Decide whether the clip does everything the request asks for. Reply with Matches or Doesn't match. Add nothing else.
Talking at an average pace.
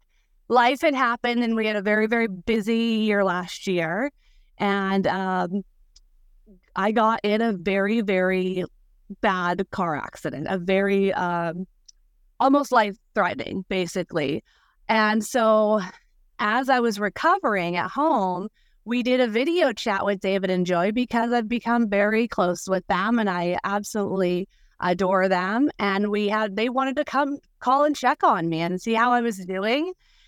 Matches